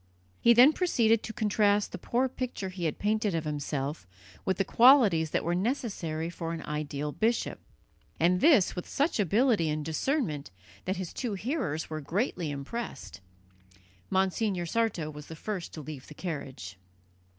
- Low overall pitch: No, medium, 185 Hz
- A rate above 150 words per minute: Yes, average, 160 wpm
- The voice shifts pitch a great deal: Yes, wide, 6.6 semitones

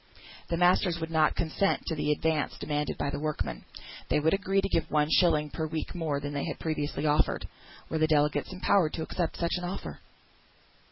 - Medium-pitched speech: Yes, medium, 160 Hz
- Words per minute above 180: Yes, average, 190 wpm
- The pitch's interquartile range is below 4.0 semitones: Yes, narrow, 2.4 semitones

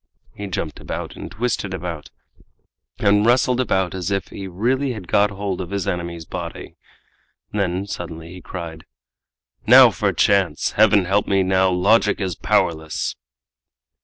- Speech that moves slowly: No, average, 145 wpm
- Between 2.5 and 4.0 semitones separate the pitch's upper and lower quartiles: Yes, average, 2.8 semitones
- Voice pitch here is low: Yes, very low, 95 Hz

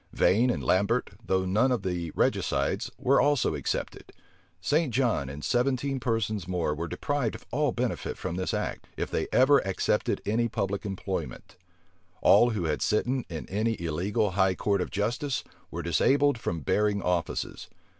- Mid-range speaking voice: No, low, 105 Hz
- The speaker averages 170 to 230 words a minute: No, average, 160 wpm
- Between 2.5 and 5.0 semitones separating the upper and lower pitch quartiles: No, wide, 5.4 semitones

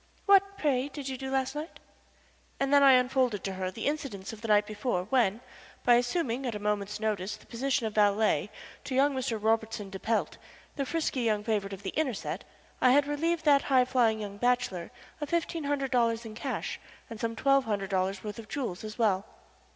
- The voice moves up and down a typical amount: Yes, average, 4.6 semitones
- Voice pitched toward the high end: Yes, high, 235 Hz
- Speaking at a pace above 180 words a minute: Yes, fast, 205 wpm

